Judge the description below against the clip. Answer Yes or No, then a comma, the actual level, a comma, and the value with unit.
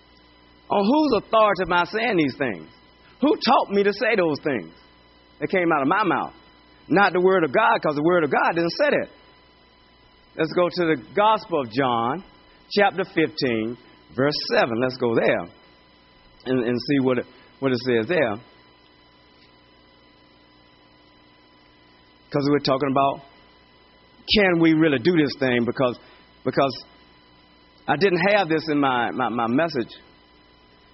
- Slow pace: No, average, 155 wpm